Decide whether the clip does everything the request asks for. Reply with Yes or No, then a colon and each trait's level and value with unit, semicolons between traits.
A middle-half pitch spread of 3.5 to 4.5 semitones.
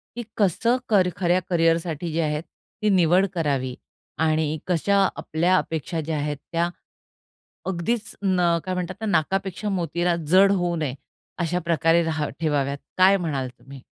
No: average, 2.9 semitones